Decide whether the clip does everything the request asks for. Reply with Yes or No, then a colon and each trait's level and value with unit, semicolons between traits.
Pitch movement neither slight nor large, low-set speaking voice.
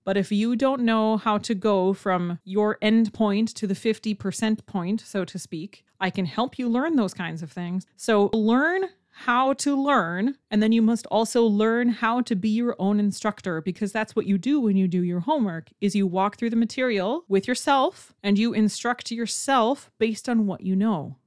No: average, 3.3 semitones; high, 215 Hz